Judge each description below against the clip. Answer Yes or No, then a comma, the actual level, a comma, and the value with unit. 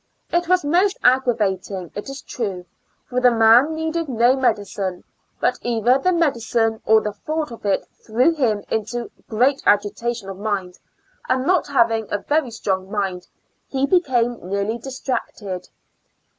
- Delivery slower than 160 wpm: Yes, average, 145 wpm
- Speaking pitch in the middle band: No, high, 235 Hz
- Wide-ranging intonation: No, average, 4.8 semitones